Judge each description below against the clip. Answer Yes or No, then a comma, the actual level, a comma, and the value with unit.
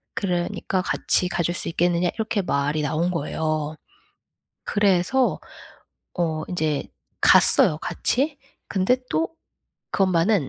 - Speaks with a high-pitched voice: No, medium, 175 Hz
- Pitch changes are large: No, average, 4.0 semitones